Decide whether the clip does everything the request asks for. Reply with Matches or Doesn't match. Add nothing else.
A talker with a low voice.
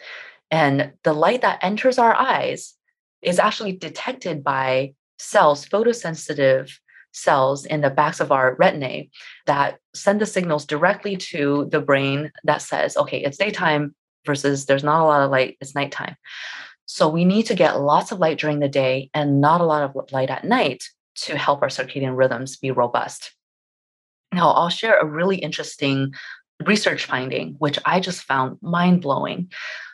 Doesn't match